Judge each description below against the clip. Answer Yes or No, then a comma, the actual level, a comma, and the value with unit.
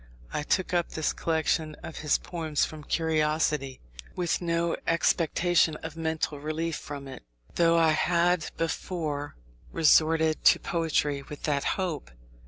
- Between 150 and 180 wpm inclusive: No, slow, 135 wpm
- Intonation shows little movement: Yes, narrow, 1.8 semitones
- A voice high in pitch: No, medium, 160 Hz